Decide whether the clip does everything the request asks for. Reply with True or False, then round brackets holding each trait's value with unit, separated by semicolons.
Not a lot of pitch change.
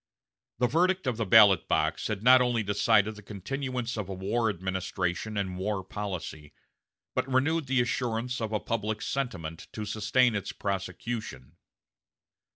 False (4.1 semitones)